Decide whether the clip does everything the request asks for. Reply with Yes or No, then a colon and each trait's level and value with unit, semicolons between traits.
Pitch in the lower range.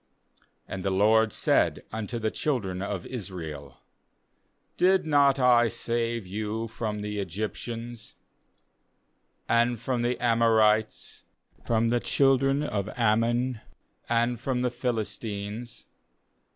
Yes: low, 115 Hz